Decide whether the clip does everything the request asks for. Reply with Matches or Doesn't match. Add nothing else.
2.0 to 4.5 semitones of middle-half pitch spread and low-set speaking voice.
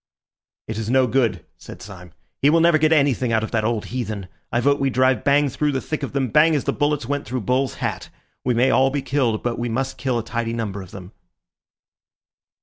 Matches